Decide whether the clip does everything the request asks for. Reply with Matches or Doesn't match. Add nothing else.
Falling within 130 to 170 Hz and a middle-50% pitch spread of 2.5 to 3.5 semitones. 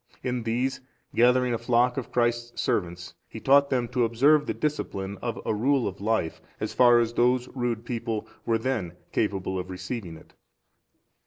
Doesn't match